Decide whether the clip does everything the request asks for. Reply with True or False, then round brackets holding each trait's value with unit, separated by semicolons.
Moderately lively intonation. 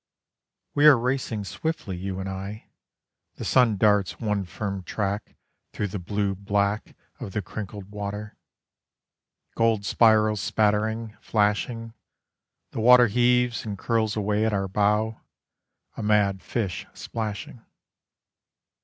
False (1.9 semitones)